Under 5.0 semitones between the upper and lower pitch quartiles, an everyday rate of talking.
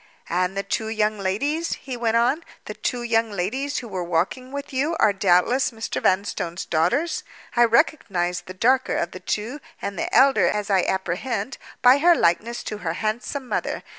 No: wide, 5.6 semitones; average, 180 wpm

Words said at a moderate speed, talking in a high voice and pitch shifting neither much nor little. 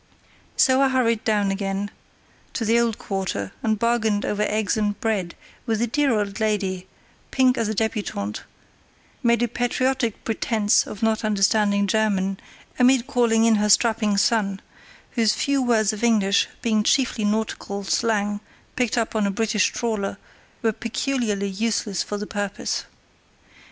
No: average, 150 wpm; high, 215 Hz; narrow, 2.3 semitones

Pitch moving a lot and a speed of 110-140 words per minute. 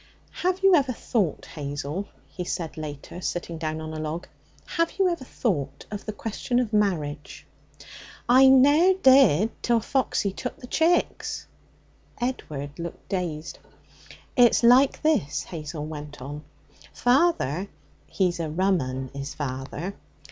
Yes: wide, 8.9 semitones; slow, 135 wpm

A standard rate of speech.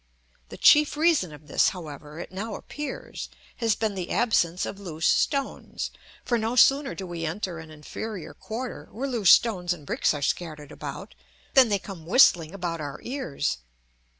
Yes: average, 170 wpm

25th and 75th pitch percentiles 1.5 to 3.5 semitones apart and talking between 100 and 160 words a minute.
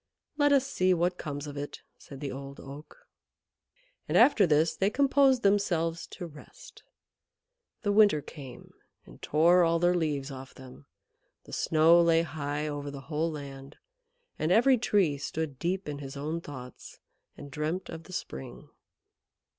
No: average, 4.3 semitones; average, 155 wpm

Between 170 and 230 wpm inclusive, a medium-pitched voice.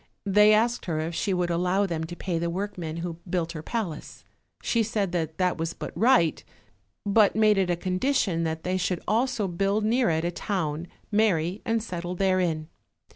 Yes: average, 185 wpm; medium, 180 Hz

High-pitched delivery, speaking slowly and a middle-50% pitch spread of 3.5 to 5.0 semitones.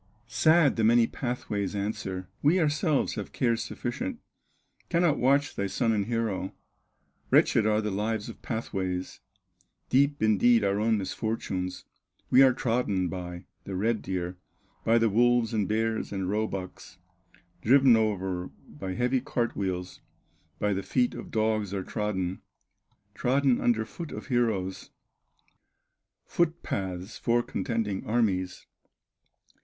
No: low, 110 Hz; slow, 130 wpm; average, 4.0 semitones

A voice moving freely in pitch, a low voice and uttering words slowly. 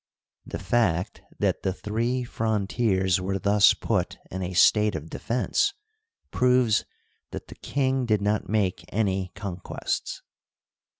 No: average, 4.0 semitones; low, 105 Hz; slow, 130 wpm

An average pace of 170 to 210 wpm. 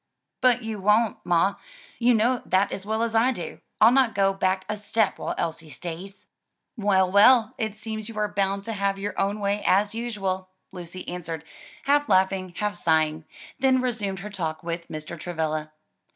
Yes: average, 180 wpm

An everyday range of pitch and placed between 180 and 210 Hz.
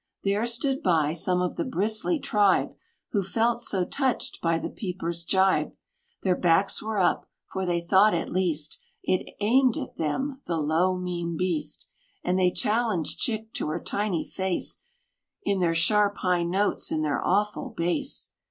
Yes: average, 3.9 semitones; medium, 185 Hz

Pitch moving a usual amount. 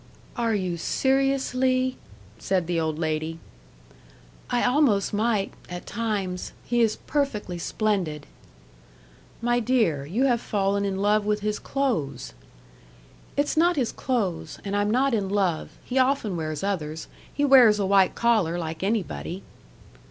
No: wide, 5.7 semitones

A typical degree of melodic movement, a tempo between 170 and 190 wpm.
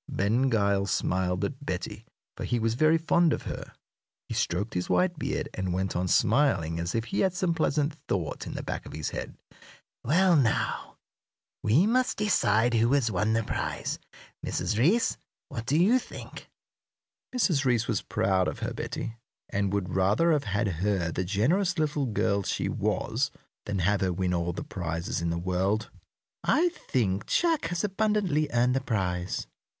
No: wide, 8.7 semitones; average, 175 wpm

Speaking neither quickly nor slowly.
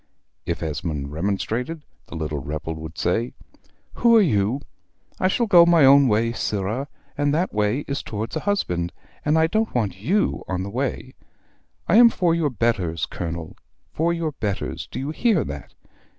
Yes: average, 170 wpm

